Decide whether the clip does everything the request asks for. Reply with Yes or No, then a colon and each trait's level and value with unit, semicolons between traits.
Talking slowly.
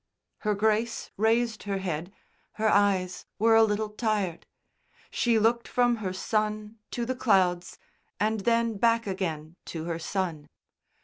No: average, 145 wpm